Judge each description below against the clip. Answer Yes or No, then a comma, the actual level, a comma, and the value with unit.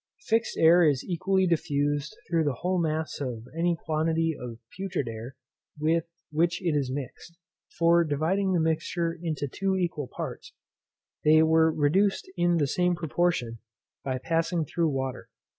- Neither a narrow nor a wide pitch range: Yes, average, 3.2 semitones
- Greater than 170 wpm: No, average, 150 wpm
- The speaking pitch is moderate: Yes, medium, 160 Hz